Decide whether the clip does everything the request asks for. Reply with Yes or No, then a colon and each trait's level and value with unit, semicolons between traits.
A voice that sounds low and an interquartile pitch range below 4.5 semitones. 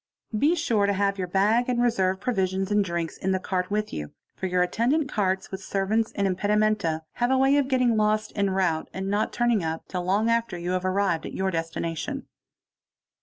No: high, 195 Hz; average, 3.4 semitones